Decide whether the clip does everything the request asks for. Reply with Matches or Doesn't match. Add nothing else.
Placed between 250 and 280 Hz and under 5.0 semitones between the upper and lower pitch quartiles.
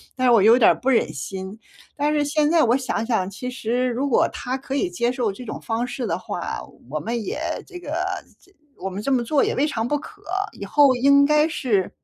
Matches